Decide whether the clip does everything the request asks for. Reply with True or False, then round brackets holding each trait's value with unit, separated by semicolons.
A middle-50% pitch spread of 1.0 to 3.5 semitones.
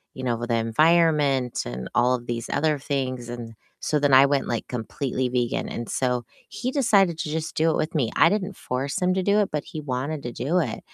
False (4.7 semitones)